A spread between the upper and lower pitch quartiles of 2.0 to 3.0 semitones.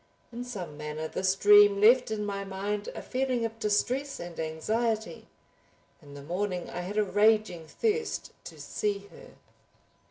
No: average, 3.9 semitones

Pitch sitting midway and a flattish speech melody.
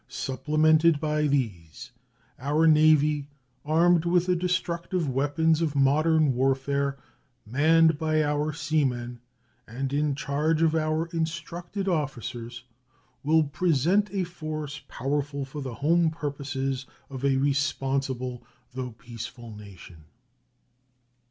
No: medium, 145 Hz; average, 3.2 semitones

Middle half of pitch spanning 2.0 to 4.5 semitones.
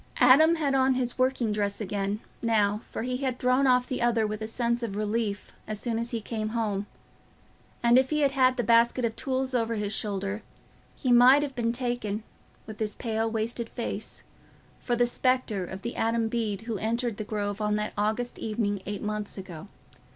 Yes: average, 2.9 semitones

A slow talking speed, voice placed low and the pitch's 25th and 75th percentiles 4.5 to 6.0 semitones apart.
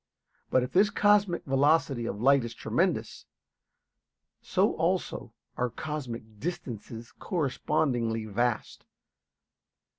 Yes: slow, 95 wpm; low, 125 Hz; average, 5.1 semitones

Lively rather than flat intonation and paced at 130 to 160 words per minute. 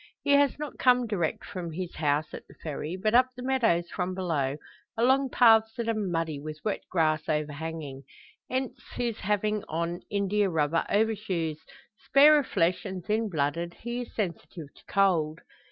No: wide, 5.7 semitones; average, 170 wpm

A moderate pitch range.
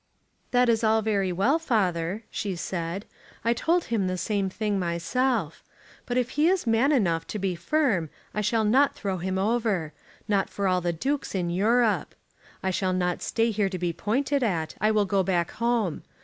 Yes: average, 4.3 semitones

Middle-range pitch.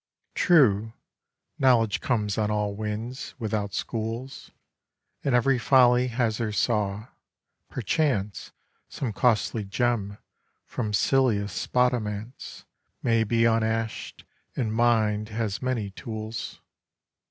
No: low, 115 Hz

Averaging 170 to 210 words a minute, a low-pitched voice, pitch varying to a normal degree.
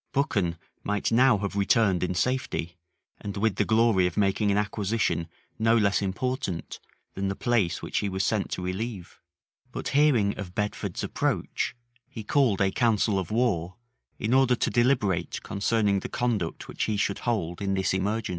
Yes: average, 175 wpm; low, 105 Hz; average, 3.3 semitones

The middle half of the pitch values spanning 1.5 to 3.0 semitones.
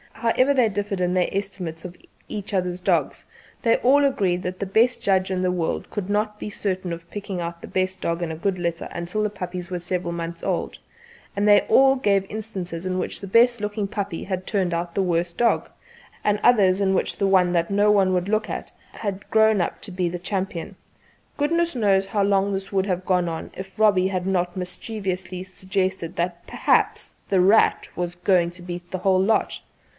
Yes: narrow, 2.4 semitones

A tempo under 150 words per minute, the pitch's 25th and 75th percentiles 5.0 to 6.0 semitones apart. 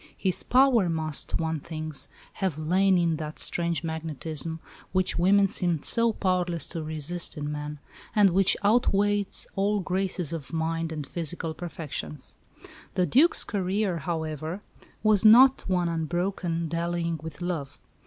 No: slow, 135 wpm; average, 3.3 semitones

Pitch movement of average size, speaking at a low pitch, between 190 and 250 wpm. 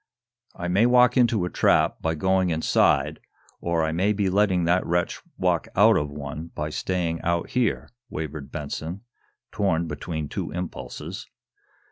No: average, 3.3 semitones; very low, 85 Hz; average, 150 wpm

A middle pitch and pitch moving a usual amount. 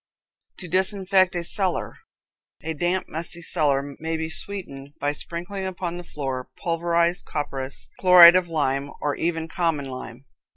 Yes: medium, 170 Hz; average, 3.7 semitones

